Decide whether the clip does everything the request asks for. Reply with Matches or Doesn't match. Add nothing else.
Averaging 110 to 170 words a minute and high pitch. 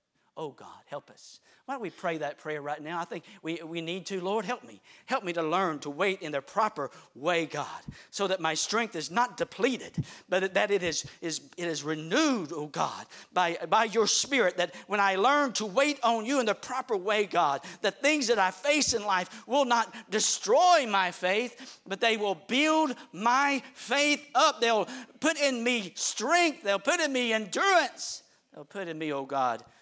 Doesn't match